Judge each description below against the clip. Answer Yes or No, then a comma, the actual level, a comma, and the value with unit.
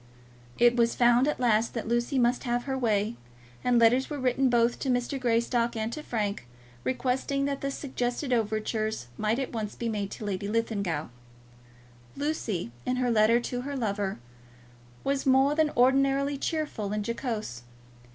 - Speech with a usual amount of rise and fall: Yes, average, 3.4 semitones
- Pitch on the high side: Yes, high, 240 Hz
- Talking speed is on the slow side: No, average, 160 wpm